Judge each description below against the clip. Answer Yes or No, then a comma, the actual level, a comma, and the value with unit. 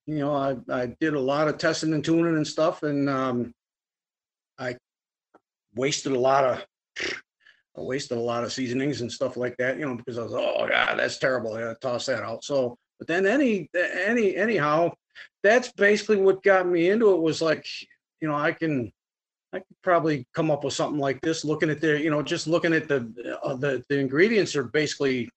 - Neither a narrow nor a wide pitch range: Yes, average, 4.1 semitones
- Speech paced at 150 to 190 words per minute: No, fast, 205 wpm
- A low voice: No, medium, 150 Hz